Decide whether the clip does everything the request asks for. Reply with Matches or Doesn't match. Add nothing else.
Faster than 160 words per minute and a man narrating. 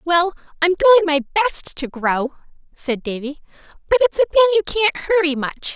Doesn't match